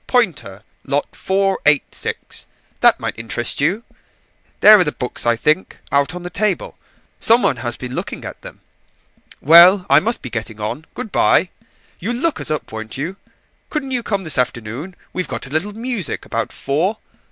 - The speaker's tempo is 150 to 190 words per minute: Yes, average, 175 wpm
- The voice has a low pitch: No, medium, 160 Hz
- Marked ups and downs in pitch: Yes, wide, 7.8 semitones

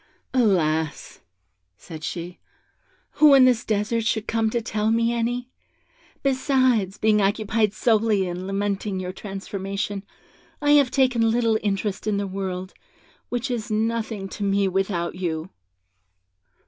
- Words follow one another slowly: Yes, slow, 130 wpm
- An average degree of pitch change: Yes, average, 3.2 semitones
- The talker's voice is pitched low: No, high, 210 Hz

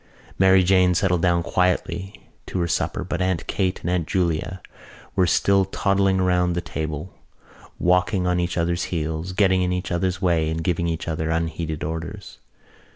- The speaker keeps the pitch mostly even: Yes, narrow, 2.0 semitones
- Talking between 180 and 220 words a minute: No, average, 165 wpm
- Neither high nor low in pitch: No, very low, 90 Hz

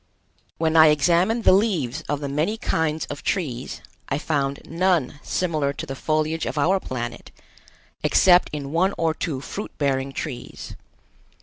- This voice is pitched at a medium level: Yes, medium, 155 Hz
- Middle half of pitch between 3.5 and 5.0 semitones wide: Yes, average, 3.9 semitones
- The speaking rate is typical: Yes, average, 150 wpm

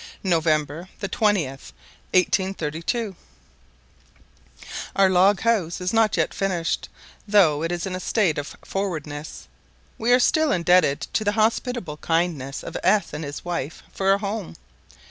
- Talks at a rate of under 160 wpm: Yes, average, 140 wpm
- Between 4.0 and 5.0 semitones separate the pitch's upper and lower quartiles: Yes, average, 4.5 semitones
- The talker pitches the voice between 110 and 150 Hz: No, medium, 180 Hz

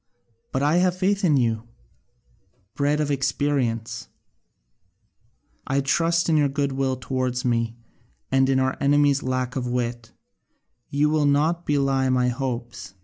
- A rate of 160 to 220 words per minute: No, slow, 135 wpm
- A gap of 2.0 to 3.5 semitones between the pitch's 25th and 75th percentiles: Yes, average, 2.7 semitones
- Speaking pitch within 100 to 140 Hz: Yes, low, 135 Hz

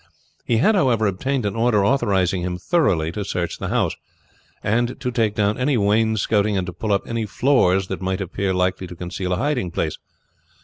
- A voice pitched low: Yes, low, 105 Hz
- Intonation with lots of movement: No, average, 4.3 semitones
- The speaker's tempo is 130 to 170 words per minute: No, average, 190 wpm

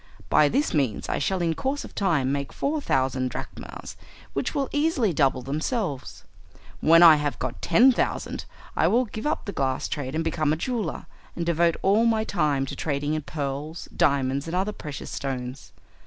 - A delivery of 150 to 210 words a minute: Yes, average, 185 wpm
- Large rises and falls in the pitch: Yes, wide, 6.6 semitones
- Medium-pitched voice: Yes, medium, 155 Hz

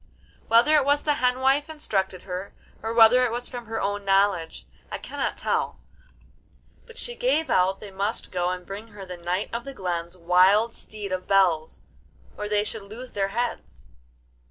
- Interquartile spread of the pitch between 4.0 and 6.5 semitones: Yes, average, 4.7 semitones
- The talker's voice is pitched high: Yes, high, 205 Hz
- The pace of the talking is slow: No, average, 180 wpm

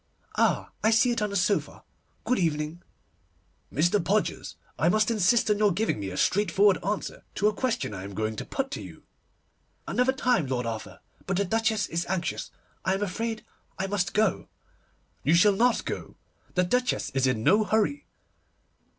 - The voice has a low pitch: No, high, 200 Hz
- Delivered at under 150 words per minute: No, average, 175 wpm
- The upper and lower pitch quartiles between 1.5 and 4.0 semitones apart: No, average, 4.7 semitones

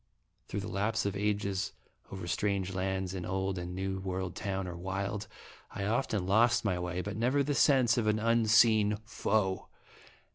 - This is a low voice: Yes, low, 100 Hz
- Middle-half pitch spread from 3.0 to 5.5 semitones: No, narrow, 2.4 semitones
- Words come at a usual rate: Yes, average, 170 wpm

